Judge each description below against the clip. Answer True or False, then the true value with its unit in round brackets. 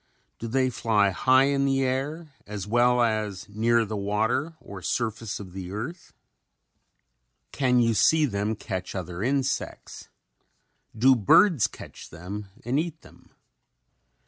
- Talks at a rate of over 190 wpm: False (135 wpm)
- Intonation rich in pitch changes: False (4.7 semitones)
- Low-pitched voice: True (115 Hz)